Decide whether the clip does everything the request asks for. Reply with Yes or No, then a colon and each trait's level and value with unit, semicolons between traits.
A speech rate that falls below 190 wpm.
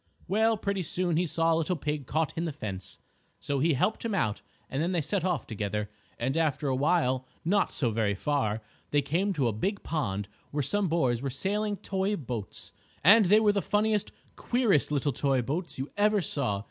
No: average, 200 wpm